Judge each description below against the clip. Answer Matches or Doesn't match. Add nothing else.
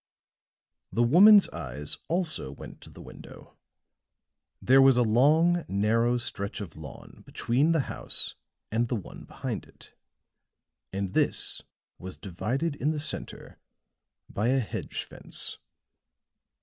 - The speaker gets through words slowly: Matches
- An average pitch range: Doesn't match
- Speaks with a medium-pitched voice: Doesn't match